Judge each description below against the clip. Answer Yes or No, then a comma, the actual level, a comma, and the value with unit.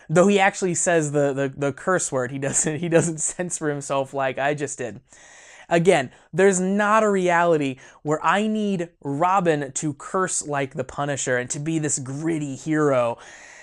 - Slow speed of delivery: No, average, 170 wpm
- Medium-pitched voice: Yes, medium, 155 Hz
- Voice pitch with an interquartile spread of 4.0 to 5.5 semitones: Yes, average, 4.3 semitones